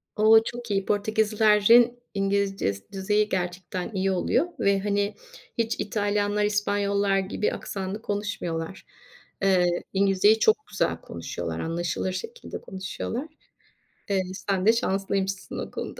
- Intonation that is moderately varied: No, narrow, 1.9 semitones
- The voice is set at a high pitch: Yes, high, 200 Hz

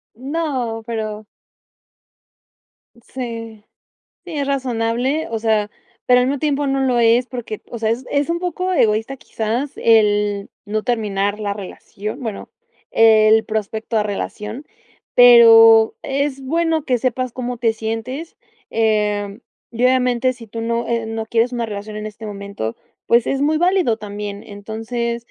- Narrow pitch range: No, average, 3.1 semitones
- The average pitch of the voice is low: No, high, 230 Hz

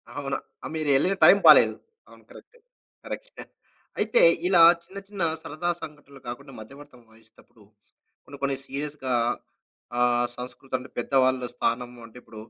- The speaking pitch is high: No, low, 135 Hz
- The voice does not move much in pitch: No, average, 3.3 semitones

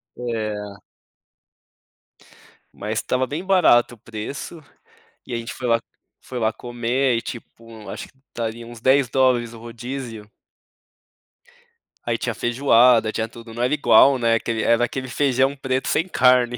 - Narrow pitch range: Yes, narrow, 2.3 semitones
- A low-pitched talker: Yes, low, 120 Hz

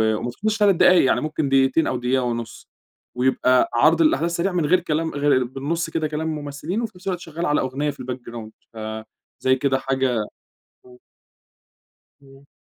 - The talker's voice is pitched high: No, medium, 140 Hz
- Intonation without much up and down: No, average, 4.2 semitones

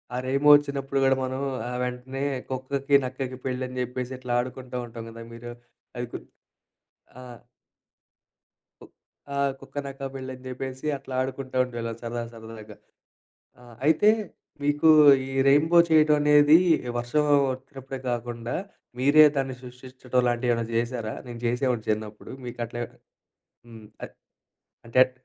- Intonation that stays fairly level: Yes, narrow, 2.1 semitones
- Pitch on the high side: No, low, 130 Hz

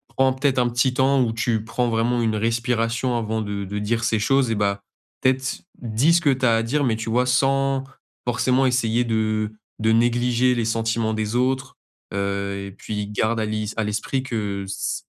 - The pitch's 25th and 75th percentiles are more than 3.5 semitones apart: No, average, 2.7 semitones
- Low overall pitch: Yes, low, 115 Hz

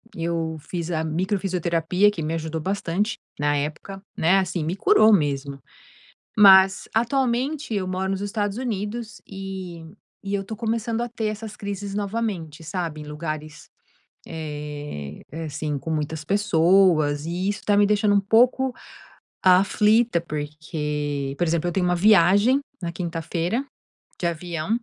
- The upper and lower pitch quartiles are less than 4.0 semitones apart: No, average, 4.5 semitones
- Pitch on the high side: No, medium, 180 Hz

